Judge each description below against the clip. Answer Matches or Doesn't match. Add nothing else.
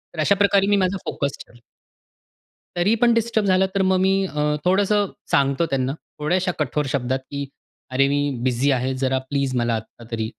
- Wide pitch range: Matches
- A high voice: Doesn't match